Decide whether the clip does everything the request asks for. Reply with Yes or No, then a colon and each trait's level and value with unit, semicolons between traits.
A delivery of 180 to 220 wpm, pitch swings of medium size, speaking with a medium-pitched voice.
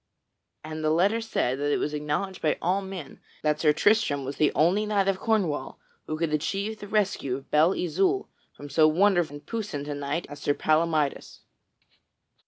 Yes: average, 185 wpm; average, 5.0 semitones; medium, 160 Hz